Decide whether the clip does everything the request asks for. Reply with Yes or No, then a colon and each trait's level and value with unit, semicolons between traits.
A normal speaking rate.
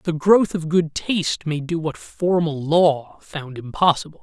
Yes: average, 170 wpm